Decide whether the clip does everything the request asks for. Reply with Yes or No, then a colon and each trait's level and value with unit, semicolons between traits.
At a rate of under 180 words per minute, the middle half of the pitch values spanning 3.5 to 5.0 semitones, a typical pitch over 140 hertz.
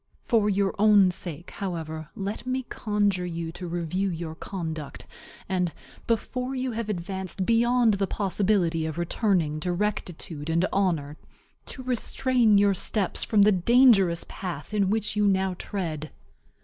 Yes: average, 145 wpm; average, 3.8 semitones; high, 190 Hz